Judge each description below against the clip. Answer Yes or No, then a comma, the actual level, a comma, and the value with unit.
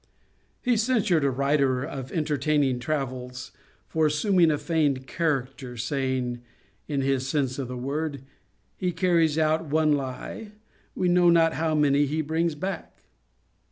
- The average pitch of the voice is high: No, medium, 150 Hz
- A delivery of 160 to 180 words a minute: No, average, 140 wpm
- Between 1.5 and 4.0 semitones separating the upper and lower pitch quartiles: Yes, average, 3.5 semitones